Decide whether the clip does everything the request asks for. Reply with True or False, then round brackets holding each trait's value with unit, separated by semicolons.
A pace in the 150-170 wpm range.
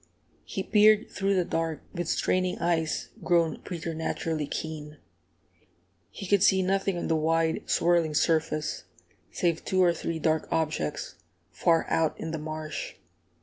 False (140 wpm)